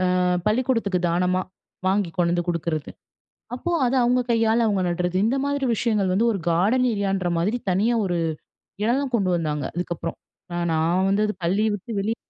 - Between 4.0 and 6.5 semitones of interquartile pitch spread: Yes, average, 4.6 semitones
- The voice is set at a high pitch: Yes, high, 195 Hz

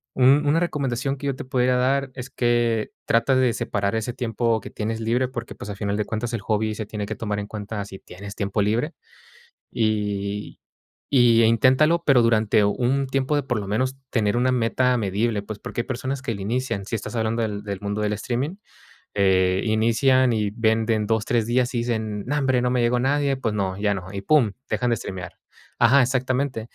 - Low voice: Yes, low, 115 Hz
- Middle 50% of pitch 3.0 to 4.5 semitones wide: Yes, average, 3.6 semitones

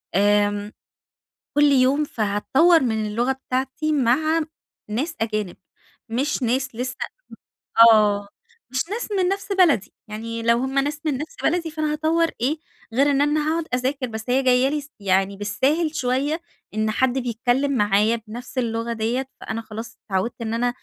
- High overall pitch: Yes, very high, 255 Hz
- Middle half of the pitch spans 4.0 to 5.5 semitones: Yes, average, 5.0 semitones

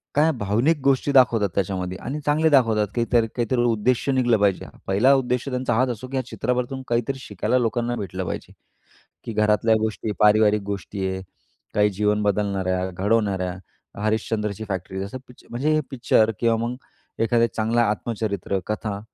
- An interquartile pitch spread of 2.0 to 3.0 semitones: No, average, 3.5 semitones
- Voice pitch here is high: No, low, 110 Hz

